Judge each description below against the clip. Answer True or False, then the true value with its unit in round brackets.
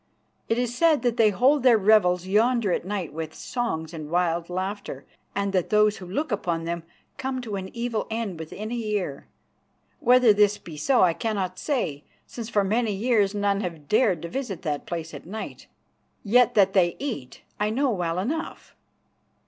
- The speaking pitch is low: False (205 Hz)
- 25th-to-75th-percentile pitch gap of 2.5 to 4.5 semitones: False (5.0 semitones)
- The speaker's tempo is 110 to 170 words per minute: False (180 wpm)